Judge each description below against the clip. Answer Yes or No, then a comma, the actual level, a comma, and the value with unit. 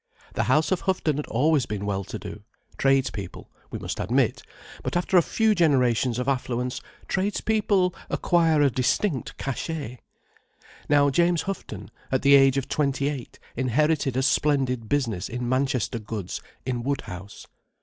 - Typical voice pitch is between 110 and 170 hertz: Yes, low, 135 Hz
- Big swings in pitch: No, average, 4.0 semitones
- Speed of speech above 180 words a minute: No, average, 150 wpm